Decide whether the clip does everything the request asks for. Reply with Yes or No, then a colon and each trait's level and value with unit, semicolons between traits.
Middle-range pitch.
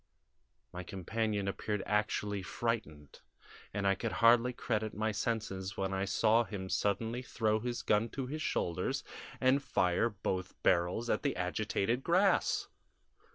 No: low, 105 Hz